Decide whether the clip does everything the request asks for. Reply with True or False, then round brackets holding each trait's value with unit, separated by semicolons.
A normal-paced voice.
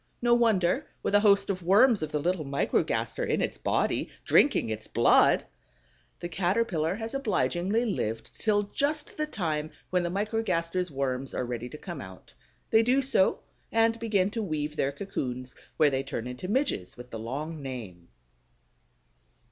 True (165 wpm)